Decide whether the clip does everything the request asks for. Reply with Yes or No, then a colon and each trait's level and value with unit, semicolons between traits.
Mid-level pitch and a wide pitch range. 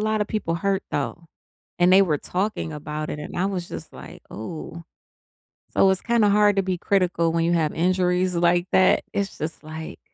No: medium, 180 Hz; average, 2.9 semitones